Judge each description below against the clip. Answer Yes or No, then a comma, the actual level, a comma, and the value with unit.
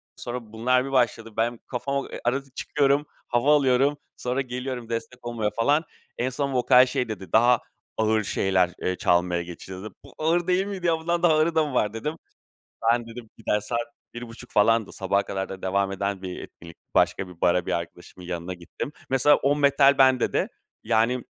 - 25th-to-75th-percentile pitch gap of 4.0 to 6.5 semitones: Yes, wide, 5.4 semitones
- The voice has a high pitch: No, low, 120 Hz